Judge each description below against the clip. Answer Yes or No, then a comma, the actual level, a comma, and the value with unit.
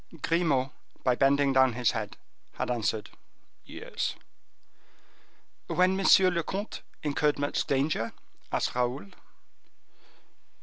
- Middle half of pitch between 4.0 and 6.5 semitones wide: Yes, average, 5.0 semitones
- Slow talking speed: Yes, slow, 100 wpm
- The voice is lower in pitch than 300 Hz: Yes, medium, 140 Hz